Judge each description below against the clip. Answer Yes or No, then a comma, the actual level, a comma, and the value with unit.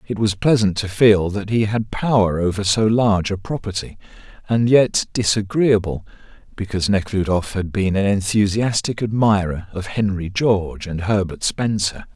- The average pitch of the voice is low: Yes, low, 100 Hz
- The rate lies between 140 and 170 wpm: Yes, average, 150 wpm